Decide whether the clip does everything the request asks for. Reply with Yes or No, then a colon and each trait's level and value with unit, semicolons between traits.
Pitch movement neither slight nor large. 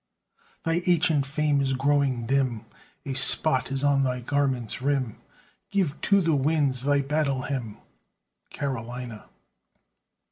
No: narrow, 2.3 semitones